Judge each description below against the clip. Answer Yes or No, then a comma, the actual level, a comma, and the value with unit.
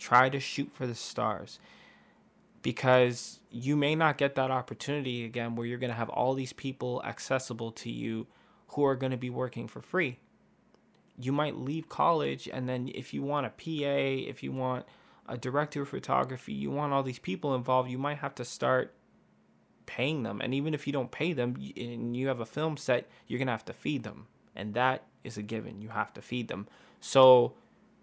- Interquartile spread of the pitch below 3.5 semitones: Yes, narrow, 2.6 semitones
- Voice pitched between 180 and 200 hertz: No, low, 130 Hz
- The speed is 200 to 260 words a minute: Yes, fast, 205 wpm